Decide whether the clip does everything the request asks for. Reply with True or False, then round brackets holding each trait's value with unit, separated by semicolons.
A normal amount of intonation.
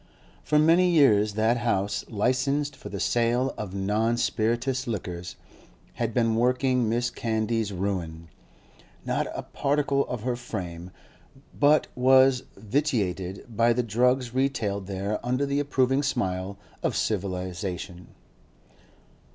True (4.6 semitones)